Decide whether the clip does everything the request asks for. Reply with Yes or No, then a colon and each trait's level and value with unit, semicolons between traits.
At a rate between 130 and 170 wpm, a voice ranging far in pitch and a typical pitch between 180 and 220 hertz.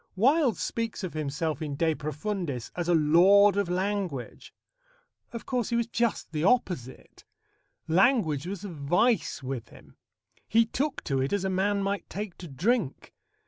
Yes: average, 160 wpm; wide, 5.7 semitones; medium, 185 Hz